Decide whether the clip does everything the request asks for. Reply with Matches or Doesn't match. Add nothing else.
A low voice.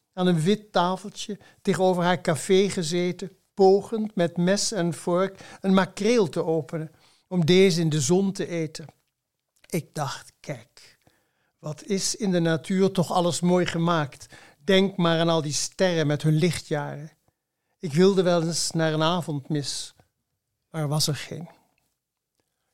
Doesn't match